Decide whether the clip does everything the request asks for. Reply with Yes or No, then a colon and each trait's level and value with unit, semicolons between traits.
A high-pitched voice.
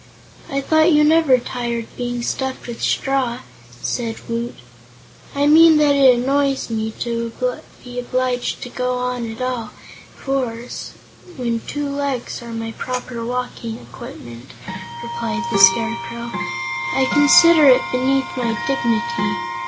Yes: high, 245 Hz